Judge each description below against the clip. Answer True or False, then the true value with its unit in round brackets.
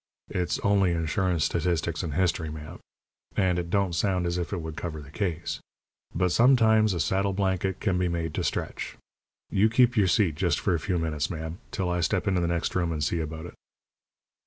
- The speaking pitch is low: True (90 Hz)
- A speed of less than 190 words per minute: False (205 wpm)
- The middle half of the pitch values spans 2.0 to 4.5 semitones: True (2.8 semitones)